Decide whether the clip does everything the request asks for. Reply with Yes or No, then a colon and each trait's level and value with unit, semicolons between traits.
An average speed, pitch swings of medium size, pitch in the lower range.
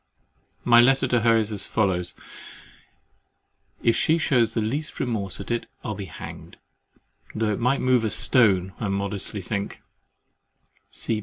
Yes: average, 145 wpm; average, 3.5 semitones; low, 110 Hz